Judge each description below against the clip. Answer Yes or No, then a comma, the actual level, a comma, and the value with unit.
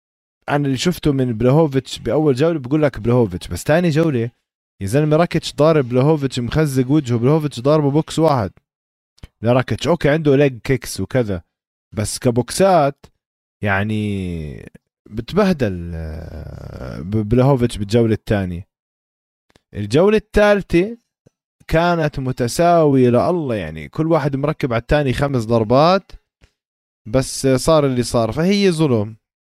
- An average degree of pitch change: No, wide, 6.7 semitones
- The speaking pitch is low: Yes, low, 130 Hz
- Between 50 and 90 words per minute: No, average, 115 wpm